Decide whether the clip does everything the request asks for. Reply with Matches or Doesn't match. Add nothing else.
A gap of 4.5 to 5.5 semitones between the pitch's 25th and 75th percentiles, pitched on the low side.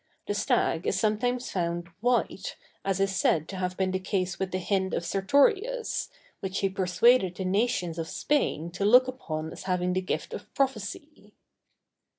Doesn't match